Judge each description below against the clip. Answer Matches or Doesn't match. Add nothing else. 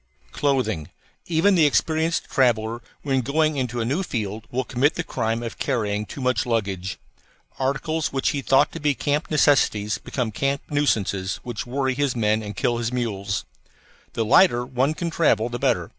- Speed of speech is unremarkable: Matches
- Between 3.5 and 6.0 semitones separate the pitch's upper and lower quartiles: Matches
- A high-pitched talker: Doesn't match